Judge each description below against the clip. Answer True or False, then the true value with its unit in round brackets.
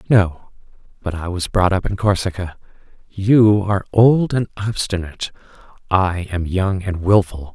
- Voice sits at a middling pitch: False (95 Hz)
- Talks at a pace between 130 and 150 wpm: True (145 wpm)